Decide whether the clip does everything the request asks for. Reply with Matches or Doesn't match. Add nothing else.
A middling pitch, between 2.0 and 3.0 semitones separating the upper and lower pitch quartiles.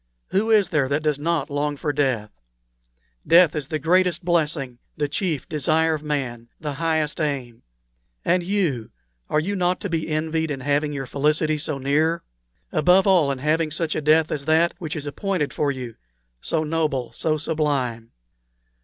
Matches